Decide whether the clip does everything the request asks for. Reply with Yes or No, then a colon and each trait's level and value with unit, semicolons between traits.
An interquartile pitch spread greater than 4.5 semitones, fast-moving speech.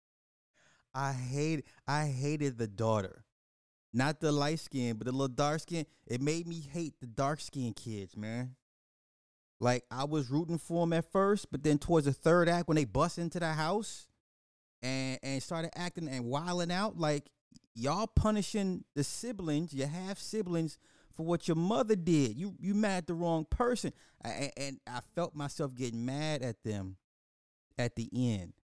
No: average, 5.1 semitones; average, 175 wpm